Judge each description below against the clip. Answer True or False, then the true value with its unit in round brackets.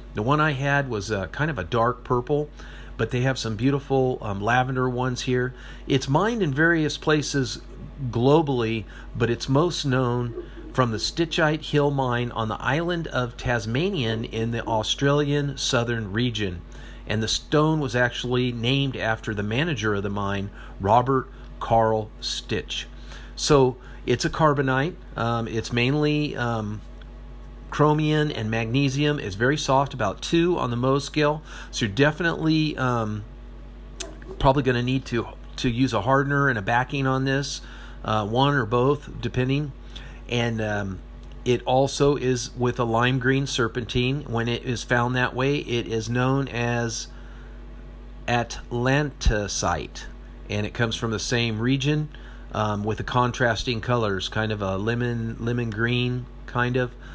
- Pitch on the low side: True (125 Hz)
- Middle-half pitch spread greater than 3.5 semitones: False (3.1 semitones)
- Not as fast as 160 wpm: True (150 wpm)